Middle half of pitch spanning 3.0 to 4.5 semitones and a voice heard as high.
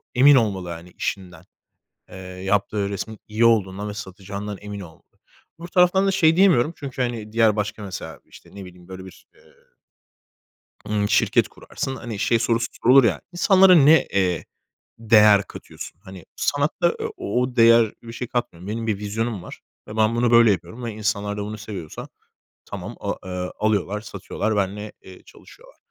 No: average, 3.3 semitones; low, 105 Hz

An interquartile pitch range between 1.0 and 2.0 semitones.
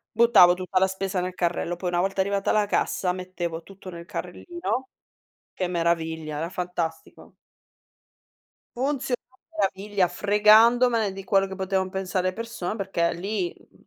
No: average, 2.9 semitones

